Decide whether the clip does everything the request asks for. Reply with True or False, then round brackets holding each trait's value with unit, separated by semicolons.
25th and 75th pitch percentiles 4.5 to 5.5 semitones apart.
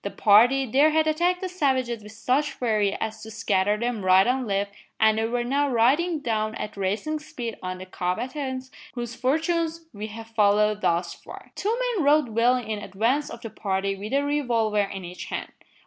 True (5.1 semitones)